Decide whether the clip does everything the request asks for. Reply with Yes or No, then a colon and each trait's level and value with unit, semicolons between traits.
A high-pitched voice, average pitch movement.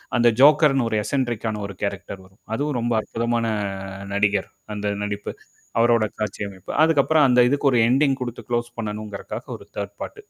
No: low, 115 Hz; average, 4.2 semitones